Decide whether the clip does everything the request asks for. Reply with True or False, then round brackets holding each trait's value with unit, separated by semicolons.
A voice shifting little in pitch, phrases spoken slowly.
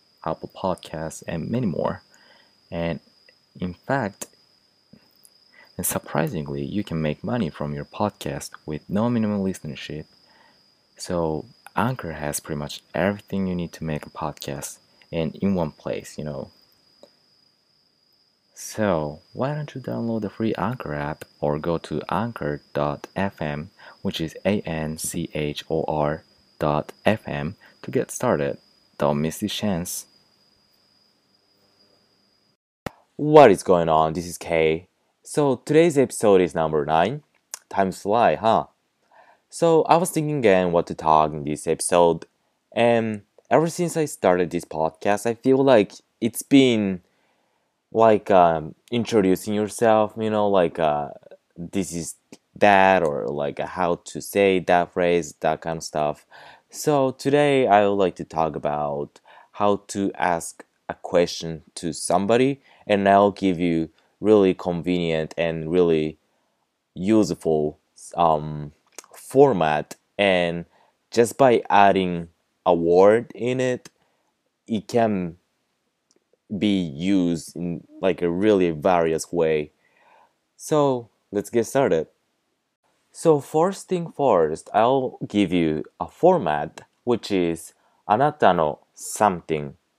False (5.0 semitones; 125 wpm)